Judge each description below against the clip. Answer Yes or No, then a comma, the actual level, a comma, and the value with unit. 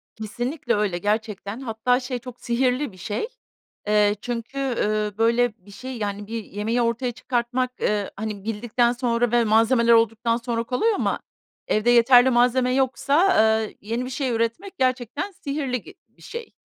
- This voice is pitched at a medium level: No, high, 235 Hz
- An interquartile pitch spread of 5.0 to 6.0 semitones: No, narrow, 2.6 semitones